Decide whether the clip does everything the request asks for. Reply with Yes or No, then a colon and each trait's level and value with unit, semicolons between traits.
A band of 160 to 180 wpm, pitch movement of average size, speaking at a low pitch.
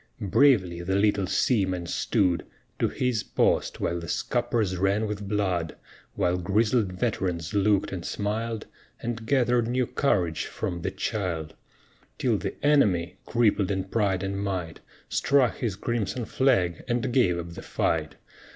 No: average, 140 wpm; average, 4.4 semitones; low, 100 Hz